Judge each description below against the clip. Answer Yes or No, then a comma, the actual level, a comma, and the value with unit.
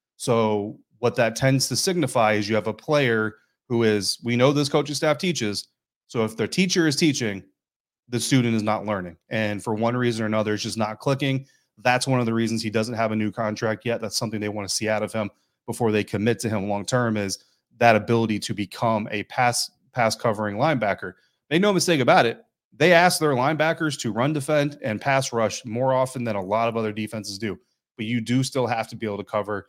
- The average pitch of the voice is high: No, low, 115 Hz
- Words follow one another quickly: Yes, fast, 225 wpm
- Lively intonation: No, average, 3.4 semitones